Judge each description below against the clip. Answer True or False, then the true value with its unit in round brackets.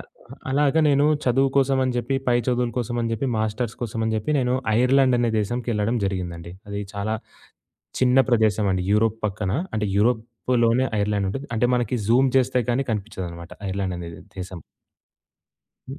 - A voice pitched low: True (115 Hz)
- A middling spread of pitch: True (3.7 semitones)